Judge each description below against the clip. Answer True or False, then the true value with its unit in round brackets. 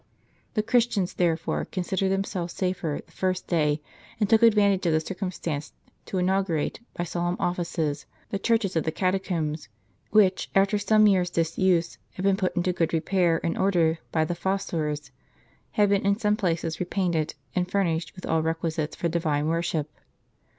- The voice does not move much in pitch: False (3.1 semitones)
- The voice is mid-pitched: True (180 Hz)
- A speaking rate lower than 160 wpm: False (165 wpm)